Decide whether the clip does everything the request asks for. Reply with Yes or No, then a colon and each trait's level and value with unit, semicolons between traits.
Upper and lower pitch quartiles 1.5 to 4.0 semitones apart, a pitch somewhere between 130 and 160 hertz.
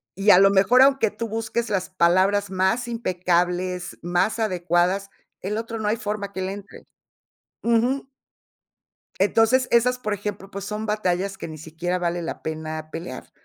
No: average, 3.7 semitones; high, 195 Hz